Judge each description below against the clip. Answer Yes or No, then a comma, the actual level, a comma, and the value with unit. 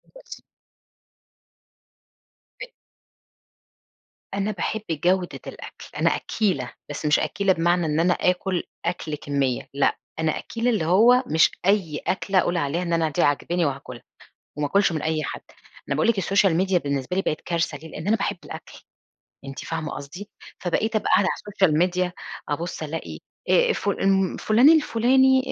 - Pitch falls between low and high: Yes, medium, 175 Hz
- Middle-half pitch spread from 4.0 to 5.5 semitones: Yes, average, 4.6 semitones